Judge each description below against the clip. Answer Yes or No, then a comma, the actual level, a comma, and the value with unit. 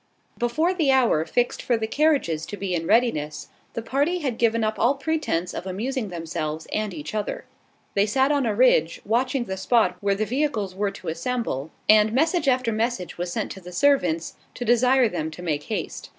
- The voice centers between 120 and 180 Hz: No, high, 220 Hz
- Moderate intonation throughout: No, wide, 6.3 semitones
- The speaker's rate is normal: Yes, average, 195 wpm